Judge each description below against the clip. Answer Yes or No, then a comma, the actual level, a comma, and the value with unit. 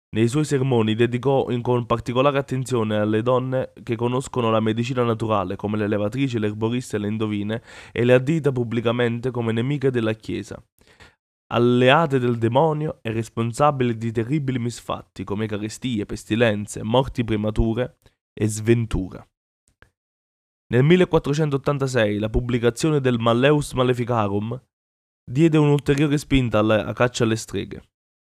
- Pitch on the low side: Yes, low, 120 Hz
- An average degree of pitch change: Yes, average, 3.0 semitones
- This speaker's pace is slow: Yes, slow, 125 wpm